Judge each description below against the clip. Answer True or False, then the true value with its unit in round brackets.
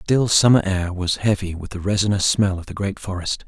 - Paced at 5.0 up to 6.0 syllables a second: True (5.5 syllables/s)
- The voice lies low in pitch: True (95 Hz)